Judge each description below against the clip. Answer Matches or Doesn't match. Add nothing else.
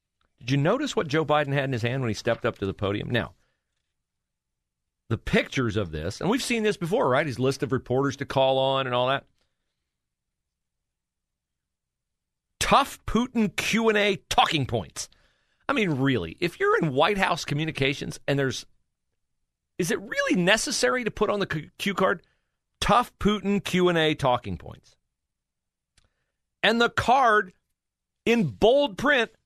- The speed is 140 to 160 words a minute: Matches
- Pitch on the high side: Doesn't match